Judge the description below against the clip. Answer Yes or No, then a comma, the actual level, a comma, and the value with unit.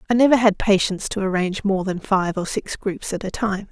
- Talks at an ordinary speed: No, fast, 240 wpm